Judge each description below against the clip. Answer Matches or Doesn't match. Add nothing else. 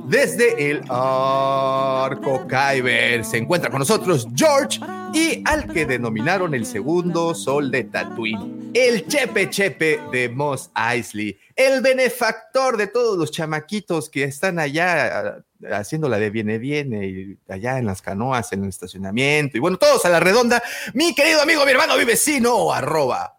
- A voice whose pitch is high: Doesn't match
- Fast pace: Doesn't match